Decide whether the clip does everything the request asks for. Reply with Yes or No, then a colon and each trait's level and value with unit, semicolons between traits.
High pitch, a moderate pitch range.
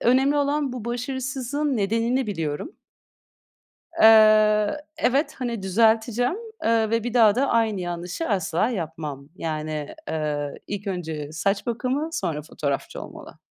No: high, 220 Hz; wide, 6.9 semitones